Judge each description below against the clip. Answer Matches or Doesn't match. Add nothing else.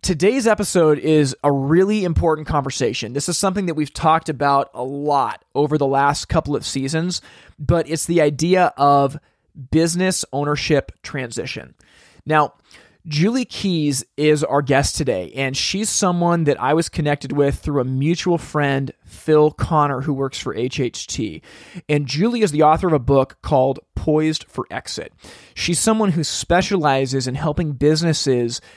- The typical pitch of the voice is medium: Matches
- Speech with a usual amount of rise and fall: Matches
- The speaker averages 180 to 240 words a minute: Doesn't match